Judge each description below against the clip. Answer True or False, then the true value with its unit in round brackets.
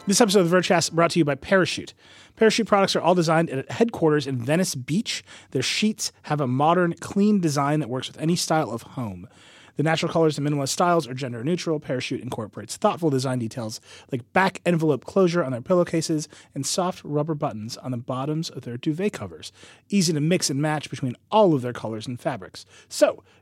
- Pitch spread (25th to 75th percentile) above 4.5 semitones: True (5.2 semitones)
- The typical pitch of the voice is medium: True (155 Hz)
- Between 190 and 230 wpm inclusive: True (200 wpm)